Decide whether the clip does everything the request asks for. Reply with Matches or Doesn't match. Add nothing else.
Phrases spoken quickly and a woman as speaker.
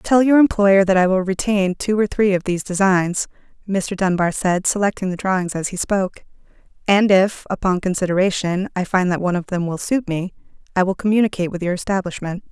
Doesn't match